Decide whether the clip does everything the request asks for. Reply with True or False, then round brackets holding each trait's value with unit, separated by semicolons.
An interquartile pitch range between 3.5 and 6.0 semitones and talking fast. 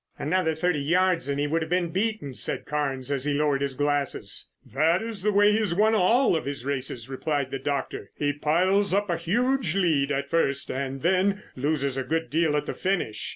True (5.0 semitones; 210 wpm)